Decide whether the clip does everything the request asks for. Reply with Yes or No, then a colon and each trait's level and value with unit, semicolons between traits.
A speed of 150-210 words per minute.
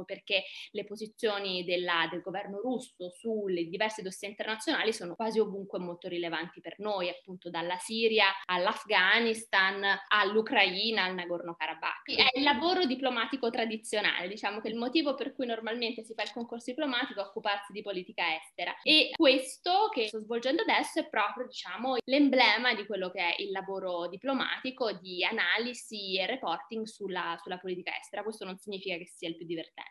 Yes: average, 160 wpm